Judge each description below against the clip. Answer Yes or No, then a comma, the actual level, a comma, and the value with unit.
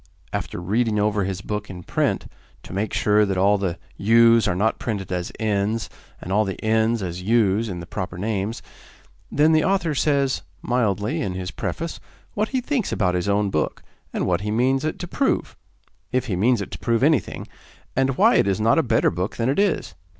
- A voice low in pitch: Yes, low, 110 Hz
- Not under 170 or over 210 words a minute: Yes, fast, 205 wpm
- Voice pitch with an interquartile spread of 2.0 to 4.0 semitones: No, average, 4.6 semitones